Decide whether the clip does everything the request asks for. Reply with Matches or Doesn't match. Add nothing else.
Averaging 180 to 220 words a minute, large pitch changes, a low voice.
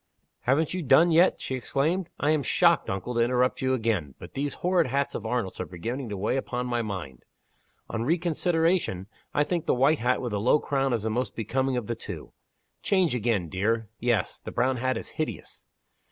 Doesn't match